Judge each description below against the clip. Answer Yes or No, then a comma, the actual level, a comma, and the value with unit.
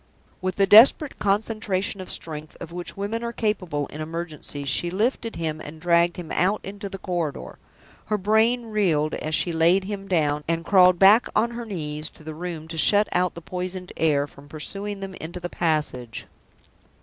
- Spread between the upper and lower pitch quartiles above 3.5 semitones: Yes, average, 4.3 semitones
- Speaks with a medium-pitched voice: Yes, medium, 180 Hz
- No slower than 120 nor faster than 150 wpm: No, average, 185 wpm